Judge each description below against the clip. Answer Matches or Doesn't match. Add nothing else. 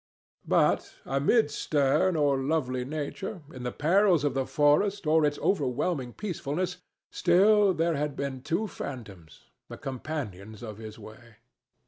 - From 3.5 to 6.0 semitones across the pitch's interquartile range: Matches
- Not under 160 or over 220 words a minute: Doesn't match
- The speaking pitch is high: Doesn't match